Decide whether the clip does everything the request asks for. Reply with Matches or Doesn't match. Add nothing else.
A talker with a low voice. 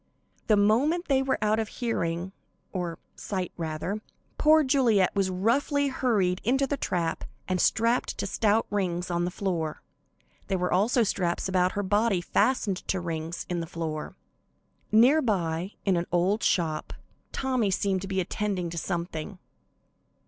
Doesn't match